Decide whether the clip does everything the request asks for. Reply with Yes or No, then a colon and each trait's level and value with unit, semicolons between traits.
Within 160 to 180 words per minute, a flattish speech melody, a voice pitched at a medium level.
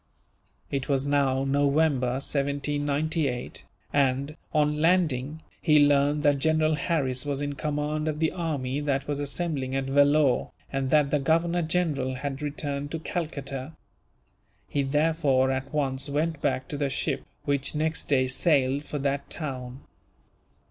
No: average, 140 wpm; narrow, 2.1 semitones; medium, 145 Hz